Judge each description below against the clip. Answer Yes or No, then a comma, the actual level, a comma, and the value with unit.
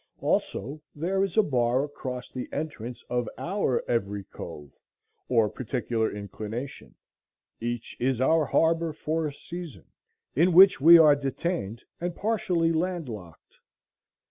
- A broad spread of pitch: Yes, wide, 5.9 semitones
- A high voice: No, medium, 140 Hz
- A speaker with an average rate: No, slow, 130 wpm